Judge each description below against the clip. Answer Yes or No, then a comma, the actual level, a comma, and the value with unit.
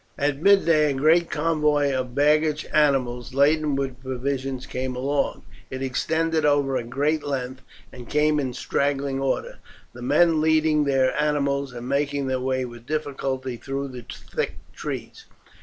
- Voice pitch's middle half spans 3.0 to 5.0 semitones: No, narrow, 2.4 semitones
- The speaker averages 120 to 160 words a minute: Yes, average, 150 wpm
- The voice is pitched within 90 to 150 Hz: Yes, medium, 140 Hz